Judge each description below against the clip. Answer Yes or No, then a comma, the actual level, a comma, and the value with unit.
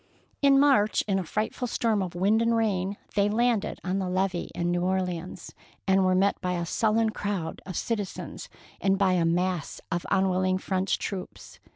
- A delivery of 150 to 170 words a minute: No, average, 180 wpm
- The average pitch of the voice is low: No, high, 190 Hz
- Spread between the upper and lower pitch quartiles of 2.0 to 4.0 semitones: Yes, average, 2.7 semitones